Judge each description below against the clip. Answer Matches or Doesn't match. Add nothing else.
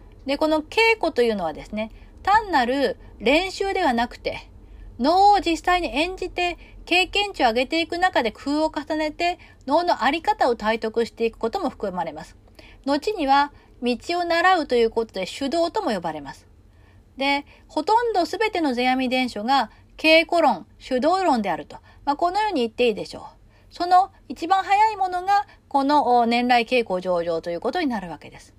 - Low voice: Doesn't match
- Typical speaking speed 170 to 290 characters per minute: Doesn't match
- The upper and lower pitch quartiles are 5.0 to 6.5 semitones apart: Doesn't match